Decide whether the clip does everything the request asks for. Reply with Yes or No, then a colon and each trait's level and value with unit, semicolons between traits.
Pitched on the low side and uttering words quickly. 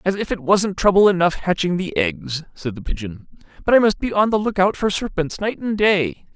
No: medium, 180 Hz; fast, 235 wpm